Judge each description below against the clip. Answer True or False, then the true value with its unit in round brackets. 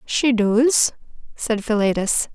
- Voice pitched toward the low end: False (225 Hz)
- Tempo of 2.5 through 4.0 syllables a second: True (3.4 syllables/s)